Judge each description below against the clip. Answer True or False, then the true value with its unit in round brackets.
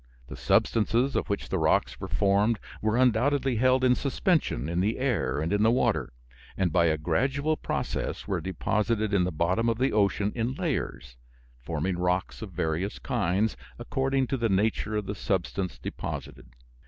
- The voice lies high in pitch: False (105 Hz)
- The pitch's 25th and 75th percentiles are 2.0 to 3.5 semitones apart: False (5.4 semitones)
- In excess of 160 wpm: True (170 wpm)